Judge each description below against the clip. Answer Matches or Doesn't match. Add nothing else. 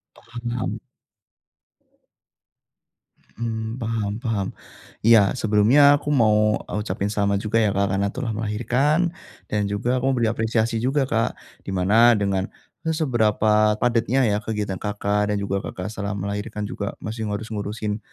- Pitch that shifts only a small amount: Matches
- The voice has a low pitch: Matches